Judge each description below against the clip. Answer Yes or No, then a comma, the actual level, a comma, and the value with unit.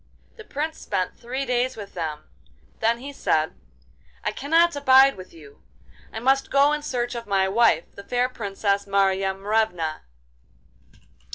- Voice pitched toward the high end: Yes, high, 230 Hz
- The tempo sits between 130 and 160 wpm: Yes, average, 150 wpm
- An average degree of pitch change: No, wide, 5.7 semitones